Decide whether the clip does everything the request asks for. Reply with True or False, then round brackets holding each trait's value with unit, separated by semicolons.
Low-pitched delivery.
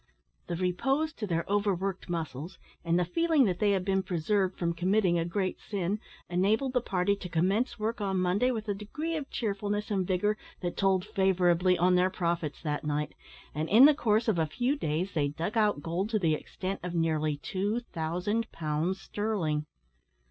False (185 Hz)